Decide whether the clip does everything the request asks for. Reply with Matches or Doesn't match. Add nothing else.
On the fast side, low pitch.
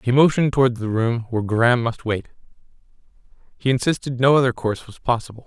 Doesn't match